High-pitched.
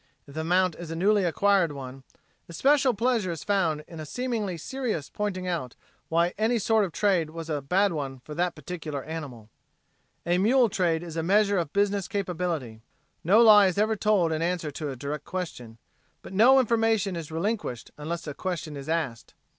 No: medium, 175 Hz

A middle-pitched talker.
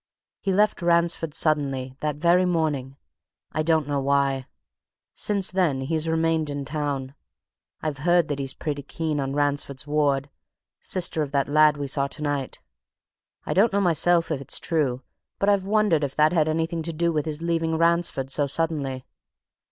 Yes: medium, 155 Hz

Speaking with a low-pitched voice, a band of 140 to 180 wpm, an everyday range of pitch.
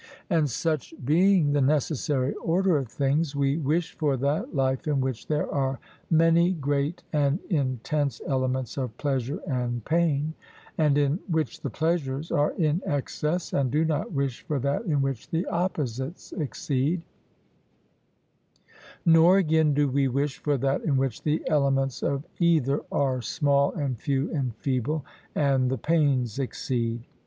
No: medium, 145 Hz; average, 150 wpm; average, 3.0 semitones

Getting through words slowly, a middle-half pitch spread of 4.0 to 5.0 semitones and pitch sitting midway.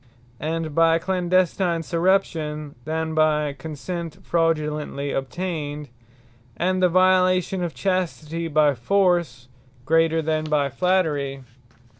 No: slow, 100 wpm; average, 3.2 semitones; medium, 165 Hz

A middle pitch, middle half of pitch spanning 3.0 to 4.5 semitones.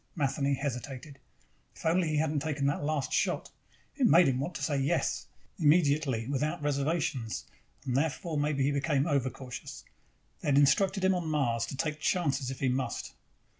No: medium, 145 Hz; narrow, 2.5 semitones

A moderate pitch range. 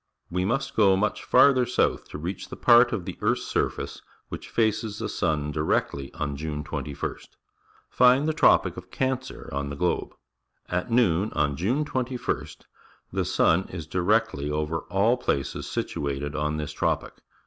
No: wide, 8.0 semitones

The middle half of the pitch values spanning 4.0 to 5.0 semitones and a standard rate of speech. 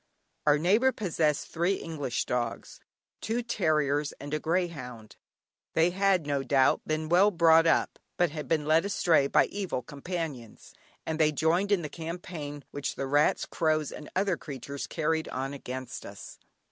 No: average, 3.5 semitones; average, 160 wpm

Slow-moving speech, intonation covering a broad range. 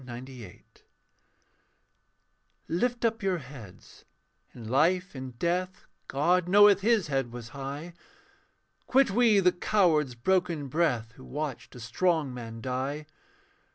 Yes: slow, 120 wpm; wide, 6.5 semitones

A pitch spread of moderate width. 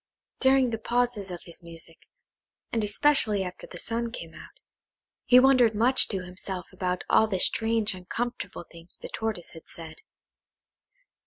Yes: average, 4.7 semitones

